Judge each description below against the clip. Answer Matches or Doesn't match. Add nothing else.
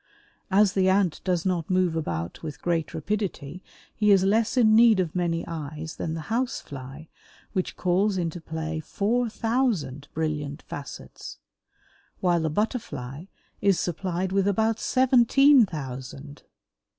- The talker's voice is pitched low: Doesn't match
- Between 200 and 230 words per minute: Doesn't match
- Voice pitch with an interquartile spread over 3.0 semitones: Matches